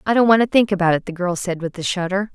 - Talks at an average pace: No, fast, 335 wpm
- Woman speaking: Yes, female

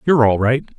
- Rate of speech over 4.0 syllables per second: Yes, 5.9 syllables/s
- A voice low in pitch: Yes, low, 125 Hz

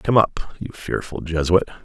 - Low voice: Yes, very low, 90 Hz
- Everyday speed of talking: Yes, average, 165 wpm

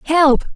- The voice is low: No, very high, 305 Hz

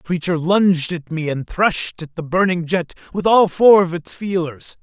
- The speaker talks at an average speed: No, fast, 210 wpm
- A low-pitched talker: No, medium, 175 Hz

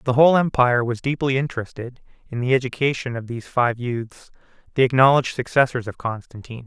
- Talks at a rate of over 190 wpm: No, average, 160 wpm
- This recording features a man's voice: Yes, male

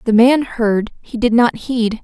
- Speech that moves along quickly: Yes, fast, 235 wpm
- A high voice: Yes, high, 230 Hz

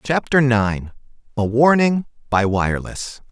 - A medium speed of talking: No, slow, 90 wpm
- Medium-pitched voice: No, low, 125 Hz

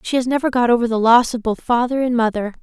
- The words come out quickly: Yes, fast, 275 wpm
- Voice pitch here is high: Yes, high, 240 Hz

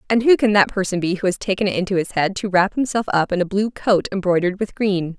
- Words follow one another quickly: Yes, fast, 280 wpm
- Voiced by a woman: Yes, female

